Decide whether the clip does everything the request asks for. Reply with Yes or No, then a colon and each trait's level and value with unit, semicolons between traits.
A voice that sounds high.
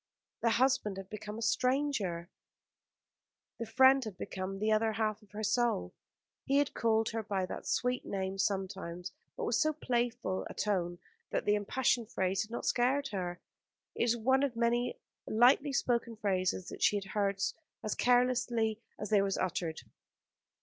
Yes: high, 220 Hz